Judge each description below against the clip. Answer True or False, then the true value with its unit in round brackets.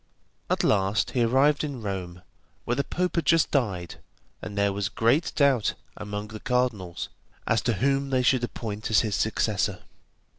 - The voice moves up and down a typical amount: True (4.7 semitones)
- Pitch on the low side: True (115 Hz)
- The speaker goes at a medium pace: True (170 wpm)